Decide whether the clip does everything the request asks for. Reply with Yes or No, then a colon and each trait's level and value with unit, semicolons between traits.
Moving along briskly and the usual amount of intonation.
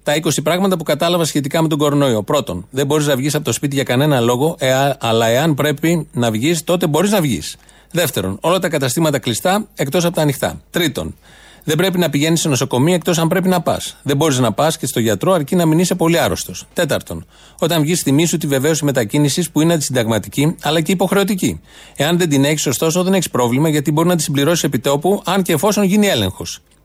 Yes: fast, 215 wpm; average, 3.8 semitones